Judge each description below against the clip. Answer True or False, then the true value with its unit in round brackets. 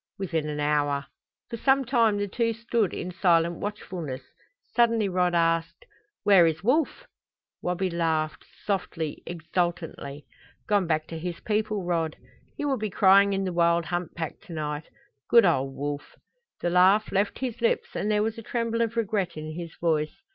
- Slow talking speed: False (170 wpm)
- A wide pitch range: False (4.8 semitones)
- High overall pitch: False (180 Hz)